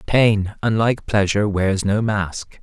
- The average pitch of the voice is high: No, low, 105 Hz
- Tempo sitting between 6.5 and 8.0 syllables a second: No, 4.2 syllables/s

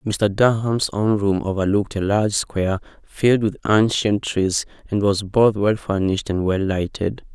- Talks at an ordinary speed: Yes, average, 165 wpm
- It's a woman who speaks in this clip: No, male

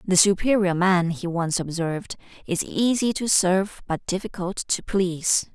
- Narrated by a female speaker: Yes, female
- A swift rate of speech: No, average, 150 wpm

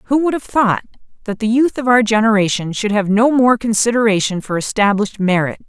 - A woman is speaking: Yes, female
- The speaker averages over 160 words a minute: Yes, average, 190 wpm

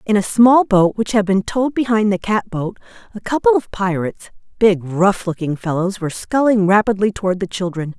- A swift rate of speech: No, average, 175 wpm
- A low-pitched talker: No, high, 200 Hz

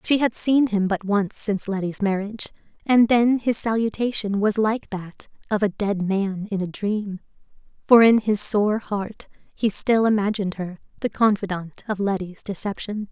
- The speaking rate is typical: Yes, average, 170 wpm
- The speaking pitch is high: Yes, high, 205 Hz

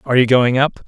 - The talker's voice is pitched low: Yes, low, 125 Hz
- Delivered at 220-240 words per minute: No, fast, 275 wpm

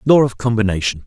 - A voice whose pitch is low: Yes, low, 110 Hz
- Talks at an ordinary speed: Yes, average, 170 wpm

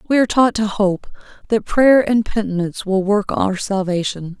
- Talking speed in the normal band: Yes, average, 175 wpm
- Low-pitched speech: No, high, 205 Hz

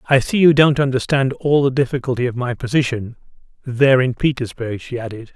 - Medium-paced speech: Yes, average, 180 wpm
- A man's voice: Yes, male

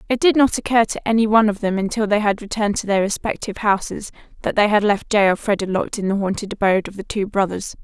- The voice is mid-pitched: No, high, 205 Hz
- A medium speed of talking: No, fast, 245 wpm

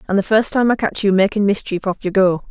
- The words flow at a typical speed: No, fast, 285 wpm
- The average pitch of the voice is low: No, high, 200 Hz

